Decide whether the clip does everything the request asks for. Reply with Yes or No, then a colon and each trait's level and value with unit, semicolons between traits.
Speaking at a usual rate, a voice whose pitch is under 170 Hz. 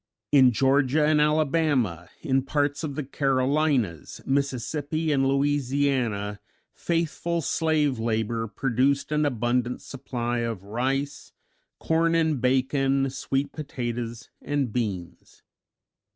No: slow, 105 wpm; low, 135 Hz